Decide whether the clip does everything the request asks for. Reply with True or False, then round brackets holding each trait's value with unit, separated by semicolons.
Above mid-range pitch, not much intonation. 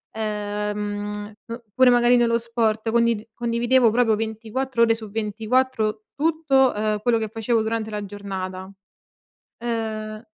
True (225 Hz; 2.1 semitones)